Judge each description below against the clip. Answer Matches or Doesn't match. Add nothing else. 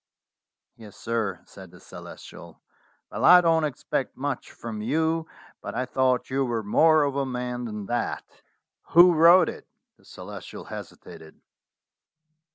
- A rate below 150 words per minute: Matches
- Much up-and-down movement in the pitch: Matches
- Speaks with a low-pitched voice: Matches